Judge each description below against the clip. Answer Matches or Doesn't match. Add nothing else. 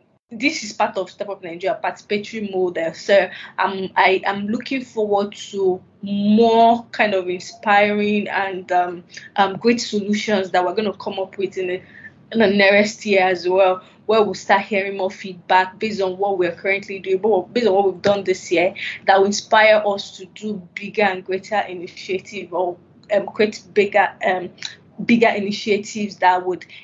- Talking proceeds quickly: Doesn't match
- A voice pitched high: Matches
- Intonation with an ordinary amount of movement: Doesn't match